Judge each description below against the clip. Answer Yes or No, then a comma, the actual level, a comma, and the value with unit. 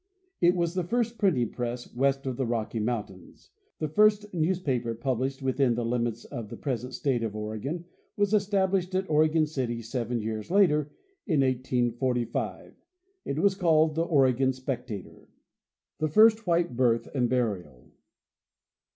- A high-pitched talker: No, low, 135 Hz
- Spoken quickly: No, average, 150 wpm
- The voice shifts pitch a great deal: Yes, wide, 6.2 semitones